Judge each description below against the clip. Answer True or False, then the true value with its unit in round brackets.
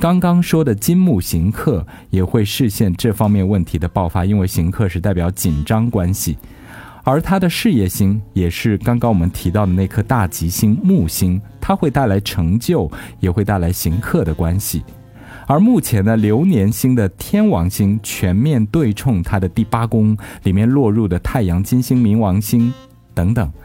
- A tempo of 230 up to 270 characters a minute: True (260 characters per minute)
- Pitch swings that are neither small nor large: True (4.7 semitones)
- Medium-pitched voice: False (105 Hz)